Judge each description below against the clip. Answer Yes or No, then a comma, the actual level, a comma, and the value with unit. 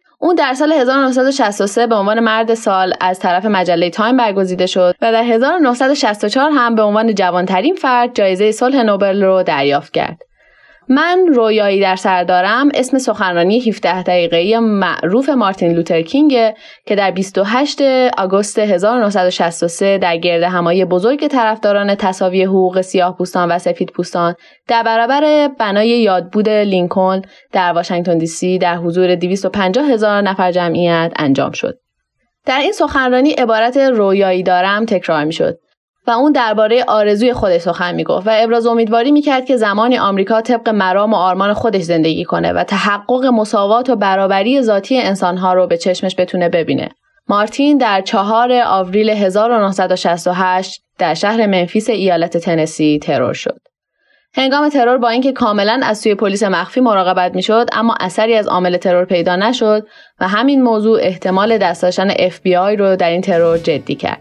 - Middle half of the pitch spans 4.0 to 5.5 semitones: Yes, average, 4.3 semitones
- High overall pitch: Yes, high, 205 Hz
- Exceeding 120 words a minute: Yes, average, 150 wpm